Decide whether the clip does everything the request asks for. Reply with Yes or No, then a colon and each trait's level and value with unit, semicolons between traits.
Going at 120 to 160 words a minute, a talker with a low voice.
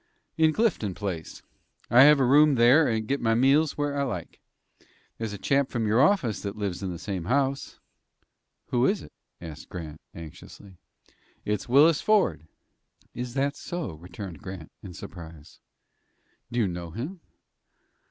Yes: average, 155 wpm; low, 115 Hz